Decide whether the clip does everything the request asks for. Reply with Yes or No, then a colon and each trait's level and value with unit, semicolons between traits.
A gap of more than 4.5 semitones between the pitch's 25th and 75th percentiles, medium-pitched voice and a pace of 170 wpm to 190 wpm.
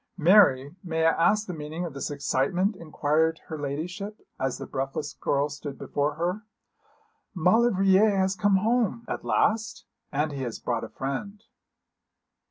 No: wide, 5.5 semitones; medium, 165 Hz; average, 150 wpm